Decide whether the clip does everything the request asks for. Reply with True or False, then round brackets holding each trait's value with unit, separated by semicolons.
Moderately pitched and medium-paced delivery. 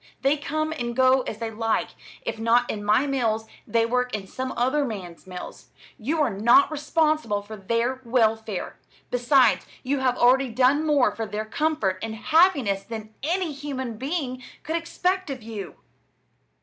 False (250 Hz; 160 wpm)